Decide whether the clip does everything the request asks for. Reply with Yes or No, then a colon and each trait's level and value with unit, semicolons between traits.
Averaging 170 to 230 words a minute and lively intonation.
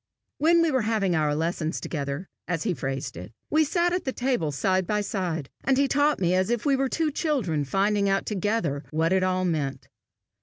Yes: fast, 205 wpm; wide, 8.6 semitones